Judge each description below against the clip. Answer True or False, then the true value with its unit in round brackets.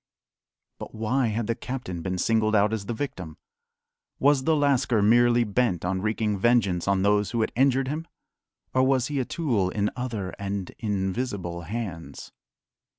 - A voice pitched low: True (110 Hz)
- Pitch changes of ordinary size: True (4.2 semitones)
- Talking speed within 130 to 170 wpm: True (160 wpm)